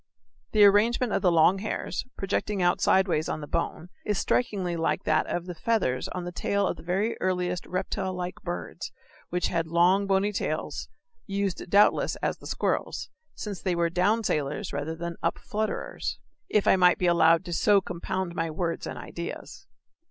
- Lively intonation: No, average, 2.8 semitones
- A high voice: No, medium, 180 Hz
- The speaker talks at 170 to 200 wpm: Yes, average, 180 wpm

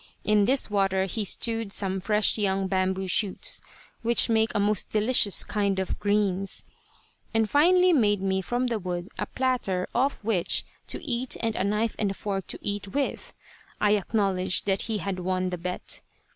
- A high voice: Yes, high, 205 Hz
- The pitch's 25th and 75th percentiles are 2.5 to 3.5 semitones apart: Yes, average, 2.9 semitones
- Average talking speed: Yes, average, 170 wpm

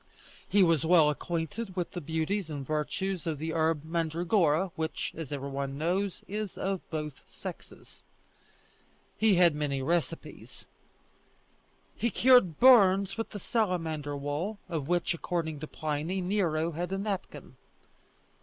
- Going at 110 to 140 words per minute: Yes, slow, 135 wpm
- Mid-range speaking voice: Yes, medium, 165 Hz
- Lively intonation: No, average, 3.8 semitones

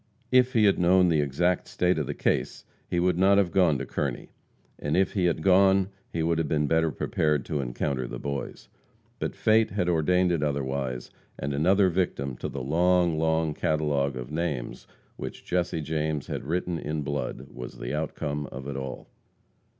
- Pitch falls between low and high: No, very low, 80 Hz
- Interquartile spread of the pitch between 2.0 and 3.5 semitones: No, average, 4.1 semitones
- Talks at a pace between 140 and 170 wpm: No, average, 185 wpm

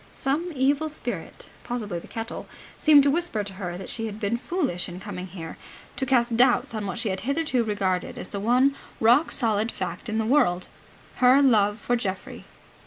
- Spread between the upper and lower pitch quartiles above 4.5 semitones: Yes, average, 5.1 semitones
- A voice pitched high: Yes, high, 230 Hz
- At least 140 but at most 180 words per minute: No, average, 190 wpm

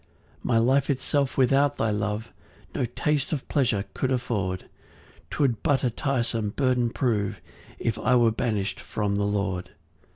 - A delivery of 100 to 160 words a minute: Yes, average, 155 wpm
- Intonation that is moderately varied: Yes, average, 4.0 semitones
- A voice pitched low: Yes, low, 120 Hz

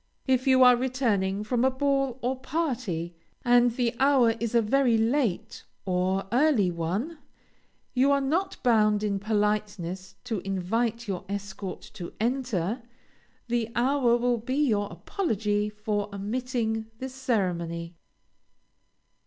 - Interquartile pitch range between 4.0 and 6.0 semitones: Yes, average, 4.3 semitones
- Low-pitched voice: No, high, 230 Hz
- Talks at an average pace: No, slow, 130 wpm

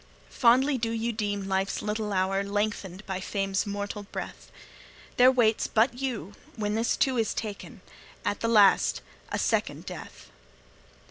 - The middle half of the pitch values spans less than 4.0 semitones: Yes, narrow, 2.6 semitones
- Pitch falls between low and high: No, high, 210 Hz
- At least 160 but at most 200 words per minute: No, average, 145 wpm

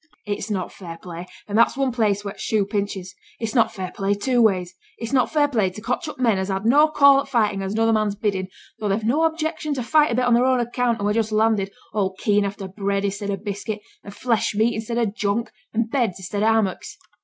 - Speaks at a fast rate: Yes, fast, 245 wpm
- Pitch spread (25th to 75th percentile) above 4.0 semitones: No, average, 3.2 semitones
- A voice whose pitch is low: No, high, 215 Hz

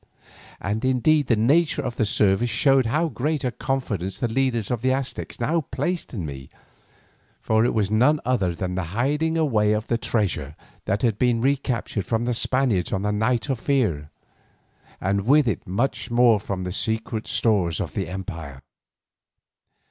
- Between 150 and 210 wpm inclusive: Yes, average, 170 wpm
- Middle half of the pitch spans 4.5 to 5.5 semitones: Yes, average, 4.9 semitones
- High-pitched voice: No, low, 115 Hz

